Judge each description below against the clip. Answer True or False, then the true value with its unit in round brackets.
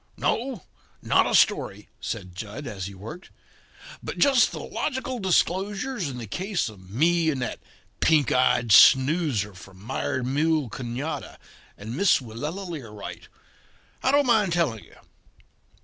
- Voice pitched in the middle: True (145 Hz)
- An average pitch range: False (8.8 semitones)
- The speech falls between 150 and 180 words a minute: False (140 wpm)